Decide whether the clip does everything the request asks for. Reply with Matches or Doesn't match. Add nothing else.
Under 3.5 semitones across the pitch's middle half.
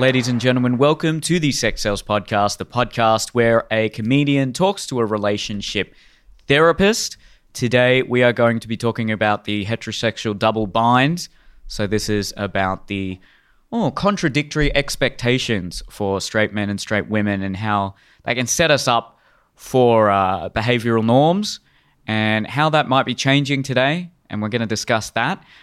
Doesn't match